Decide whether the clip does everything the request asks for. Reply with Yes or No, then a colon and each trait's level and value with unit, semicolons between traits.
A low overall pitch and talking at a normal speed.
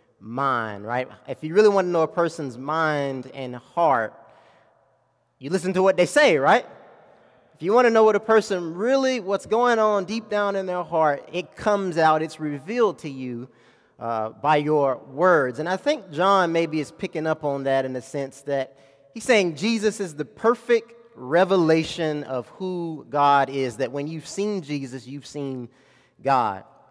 No: medium, 160 Hz; average, 180 wpm